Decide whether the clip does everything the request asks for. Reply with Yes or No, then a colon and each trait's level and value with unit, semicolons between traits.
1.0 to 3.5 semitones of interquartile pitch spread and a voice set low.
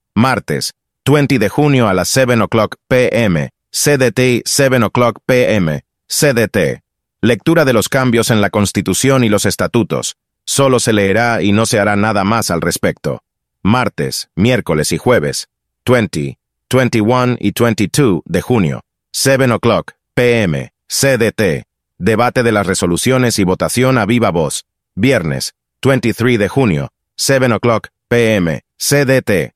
No: average, 3.9 semitones; low, 115 Hz